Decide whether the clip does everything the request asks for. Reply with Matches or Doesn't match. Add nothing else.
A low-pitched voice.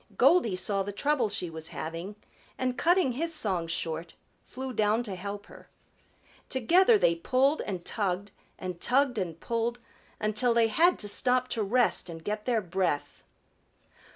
Doesn't match